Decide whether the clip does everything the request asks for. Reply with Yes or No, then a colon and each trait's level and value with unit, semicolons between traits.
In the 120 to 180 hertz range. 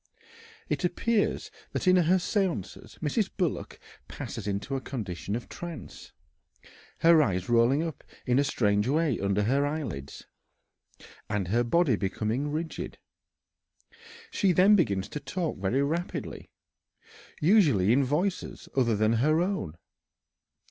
Yes: medium, 140 Hz